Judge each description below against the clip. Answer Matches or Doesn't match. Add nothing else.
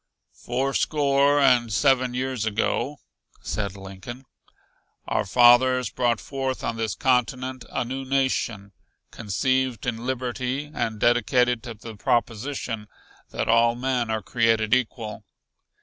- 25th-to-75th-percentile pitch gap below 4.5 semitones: Matches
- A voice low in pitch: Matches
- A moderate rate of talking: Doesn't match